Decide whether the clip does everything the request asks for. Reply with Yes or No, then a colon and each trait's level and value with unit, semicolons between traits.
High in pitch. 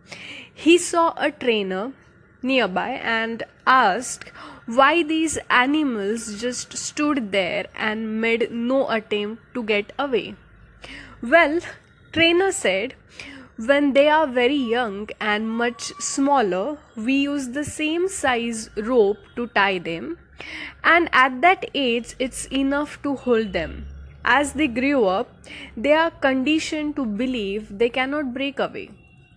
Yes: very high, 260 Hz